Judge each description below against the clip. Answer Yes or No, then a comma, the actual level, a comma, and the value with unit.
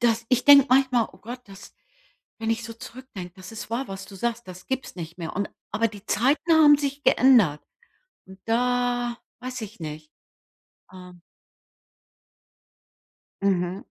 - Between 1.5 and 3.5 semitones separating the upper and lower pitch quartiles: No, average, 5.1 semitones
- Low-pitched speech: No, high, 230 Hz